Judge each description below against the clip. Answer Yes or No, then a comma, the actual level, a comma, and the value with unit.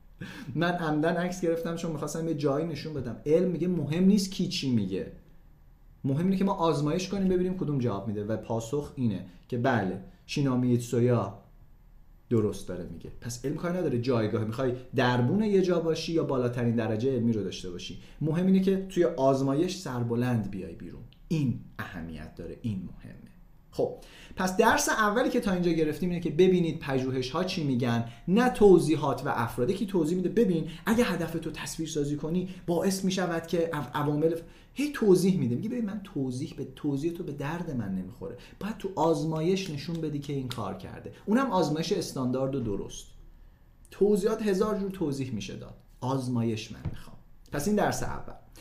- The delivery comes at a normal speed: No, fast, 175 wpm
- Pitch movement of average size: No, wide, 6.7 semitones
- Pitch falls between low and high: Yes, medium, 150 Hz